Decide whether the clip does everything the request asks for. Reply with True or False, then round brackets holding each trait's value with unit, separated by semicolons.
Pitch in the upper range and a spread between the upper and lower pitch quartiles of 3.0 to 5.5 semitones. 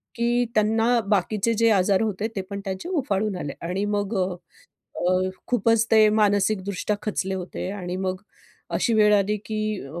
False (205 Hz; 2.4 semitones)